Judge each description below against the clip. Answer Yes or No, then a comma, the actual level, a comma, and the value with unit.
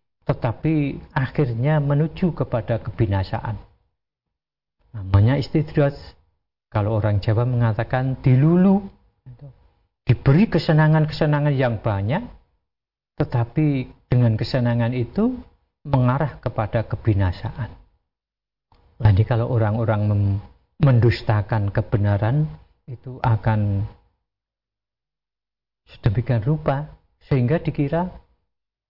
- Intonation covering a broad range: No, average, 4.9 semitones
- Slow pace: Yes, slow, 75 wpm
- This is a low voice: Yes, low, 120 Hz